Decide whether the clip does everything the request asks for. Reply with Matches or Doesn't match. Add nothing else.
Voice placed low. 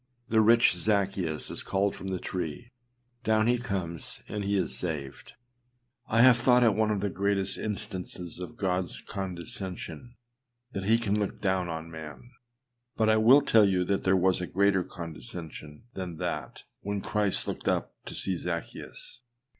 Matches